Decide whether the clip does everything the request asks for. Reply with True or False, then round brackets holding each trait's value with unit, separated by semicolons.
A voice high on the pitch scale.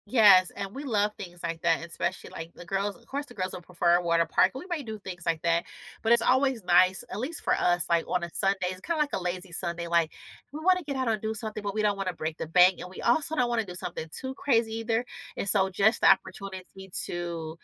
True (195 Hz)